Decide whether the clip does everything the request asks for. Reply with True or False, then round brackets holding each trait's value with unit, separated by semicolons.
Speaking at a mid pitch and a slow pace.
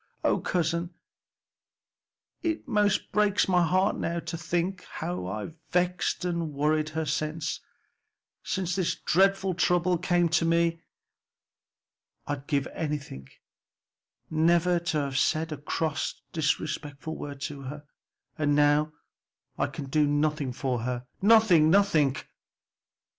True (160 Hz; 125 wpm)